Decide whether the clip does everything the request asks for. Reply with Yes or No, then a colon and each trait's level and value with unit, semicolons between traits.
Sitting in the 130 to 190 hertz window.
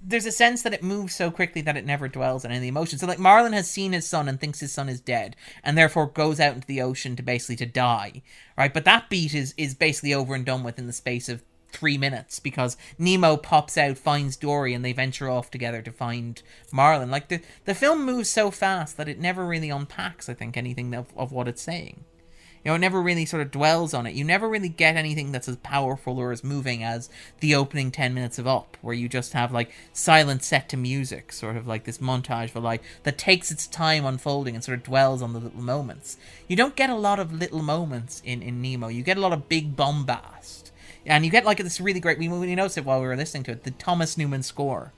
Yes: medium, 140 Hz